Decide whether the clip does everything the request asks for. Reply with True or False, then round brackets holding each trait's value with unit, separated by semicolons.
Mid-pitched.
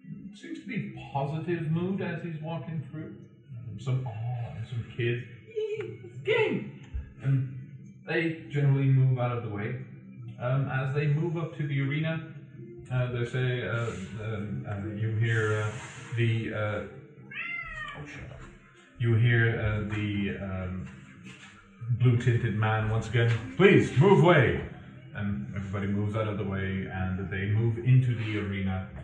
False (120 Hz)